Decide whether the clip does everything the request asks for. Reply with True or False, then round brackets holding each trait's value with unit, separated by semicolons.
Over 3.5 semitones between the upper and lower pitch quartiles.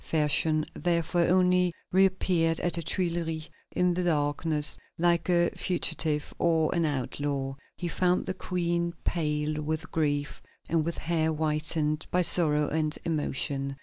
False (2.4 semitones)